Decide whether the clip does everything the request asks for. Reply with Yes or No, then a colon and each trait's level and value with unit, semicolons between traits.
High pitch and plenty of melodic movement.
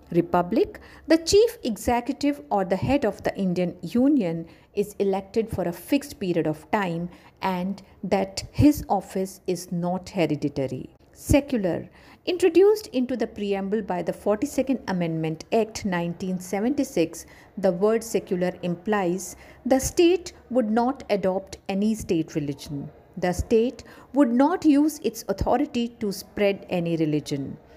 Yes: high, 200 Hz; wide, 6.2 semitones